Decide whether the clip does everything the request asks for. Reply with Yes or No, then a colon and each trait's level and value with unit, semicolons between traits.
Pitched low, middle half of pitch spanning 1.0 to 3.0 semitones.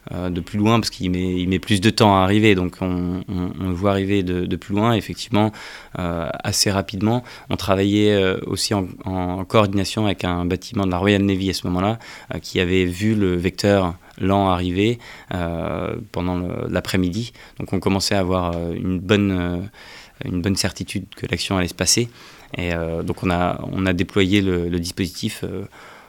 Yes: very low, 95 Hz; narrow, 2.4 semitones